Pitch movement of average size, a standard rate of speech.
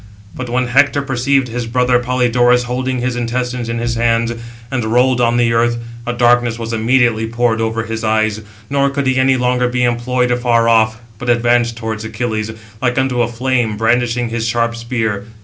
No: narrow, 1.4 semitones; average, 185 wpm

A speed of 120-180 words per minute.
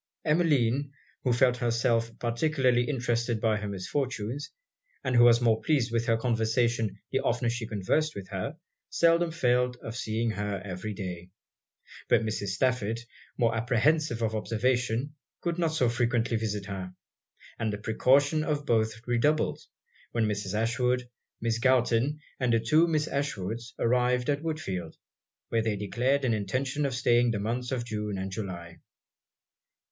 Yes: average, 150 wpm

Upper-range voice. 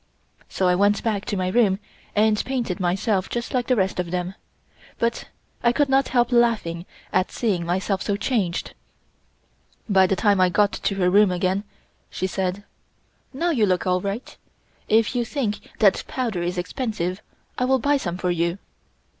Yes: high, 200 Hz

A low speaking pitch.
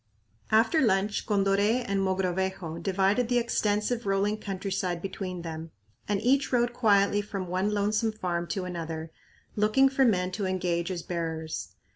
No: high, 195 Hz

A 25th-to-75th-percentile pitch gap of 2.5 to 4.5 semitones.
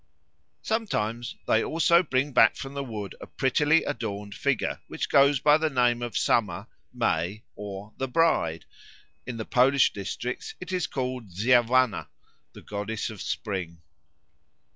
No: average, 5.0 semitones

